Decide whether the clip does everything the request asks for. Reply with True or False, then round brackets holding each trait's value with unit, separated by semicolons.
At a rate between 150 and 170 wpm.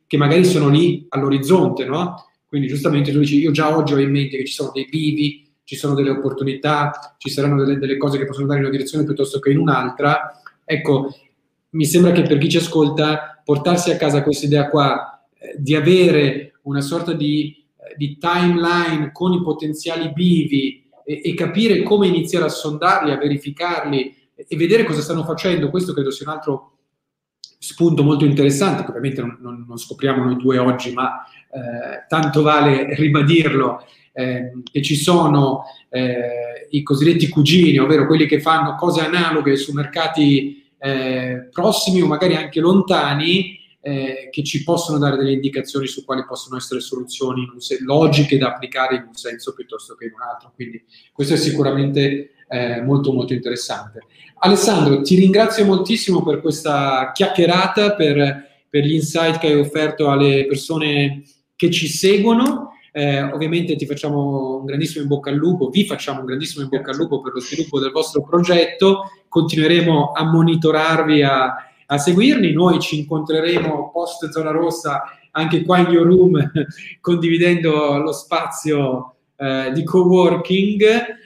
True (165 wpm)